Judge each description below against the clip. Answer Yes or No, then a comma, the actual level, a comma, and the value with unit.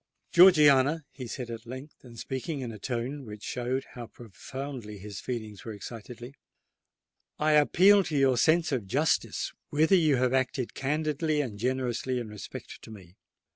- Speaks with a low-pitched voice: Yes, low, 130 Hz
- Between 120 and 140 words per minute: No, average, 155 wpm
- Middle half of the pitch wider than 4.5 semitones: No, average, 4.2 semitones